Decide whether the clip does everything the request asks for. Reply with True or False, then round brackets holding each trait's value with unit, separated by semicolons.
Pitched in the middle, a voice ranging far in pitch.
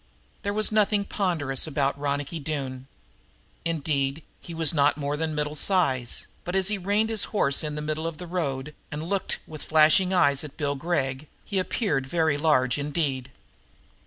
False (155 Hz; 4.0 semitones)